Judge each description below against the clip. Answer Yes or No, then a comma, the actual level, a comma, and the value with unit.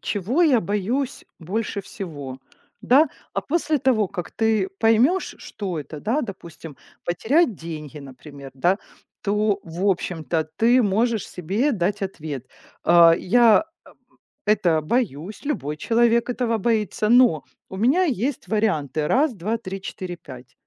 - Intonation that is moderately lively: No, wide, 6.0 semitones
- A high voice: Yes, high, 205 Hz